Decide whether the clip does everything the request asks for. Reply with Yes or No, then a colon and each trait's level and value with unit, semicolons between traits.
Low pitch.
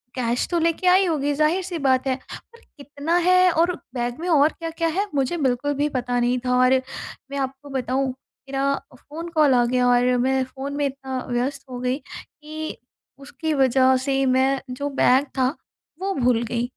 No: very high, 270 Hz